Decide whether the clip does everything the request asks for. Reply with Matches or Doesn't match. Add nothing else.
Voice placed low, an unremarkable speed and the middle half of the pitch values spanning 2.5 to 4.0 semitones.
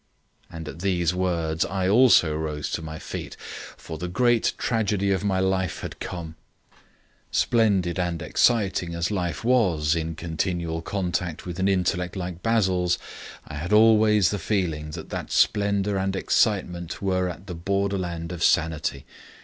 Matches